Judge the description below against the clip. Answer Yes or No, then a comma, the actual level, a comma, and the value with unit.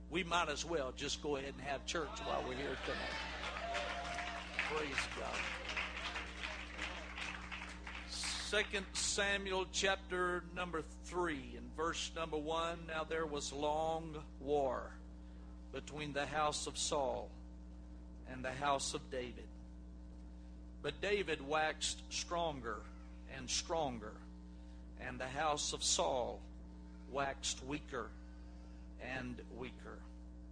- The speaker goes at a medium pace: No, slow, 110 wpm